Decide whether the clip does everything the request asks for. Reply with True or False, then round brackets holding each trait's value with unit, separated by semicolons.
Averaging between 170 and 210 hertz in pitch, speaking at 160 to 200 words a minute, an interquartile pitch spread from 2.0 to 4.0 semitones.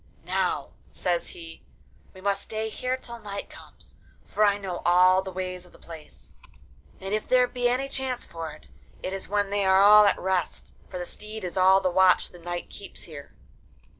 True (190 Hz; 195 wpm; 2.8 semitones)